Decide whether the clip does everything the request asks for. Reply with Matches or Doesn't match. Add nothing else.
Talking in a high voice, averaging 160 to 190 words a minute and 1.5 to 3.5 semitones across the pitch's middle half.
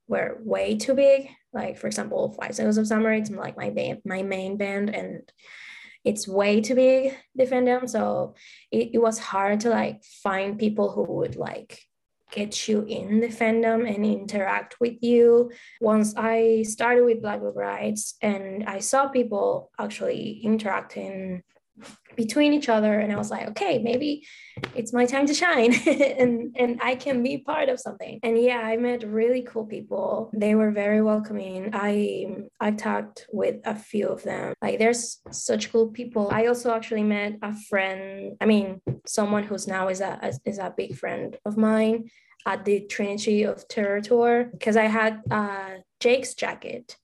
Matches